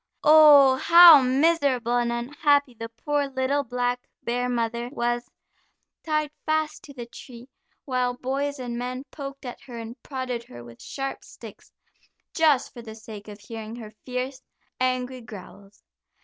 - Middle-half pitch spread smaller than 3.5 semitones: Yes, average, 2.9 semitones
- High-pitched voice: Yes, very high, 250 Hz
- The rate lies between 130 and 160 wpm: Yes, average, 150 wpm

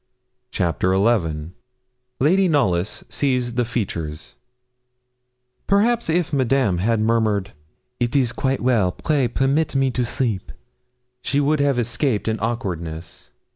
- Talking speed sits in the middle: No, slow, 120 wpm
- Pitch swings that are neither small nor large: No, wide, 6.1 semitones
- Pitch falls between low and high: No, low, 120 Hz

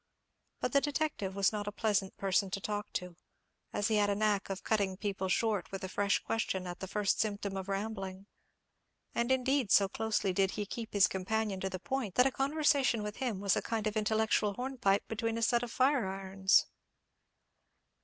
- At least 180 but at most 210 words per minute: Yes, average, 195 wpm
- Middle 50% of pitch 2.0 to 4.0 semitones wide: Yes, average, 2.8 semitones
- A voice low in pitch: No, high, 205 Hz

